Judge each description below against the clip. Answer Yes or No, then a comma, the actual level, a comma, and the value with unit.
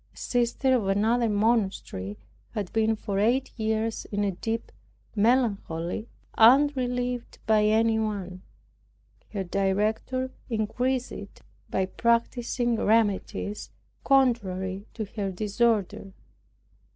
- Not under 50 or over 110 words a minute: Yes, slow, 100 wpm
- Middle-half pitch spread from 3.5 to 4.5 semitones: No, average, 3.1 semitones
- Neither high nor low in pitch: No, high, 220 Hz